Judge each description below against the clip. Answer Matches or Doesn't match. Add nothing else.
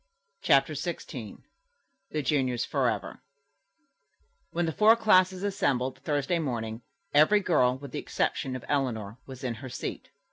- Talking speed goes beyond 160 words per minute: Doesn't match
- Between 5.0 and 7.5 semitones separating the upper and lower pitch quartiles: Matches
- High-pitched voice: Doesn't match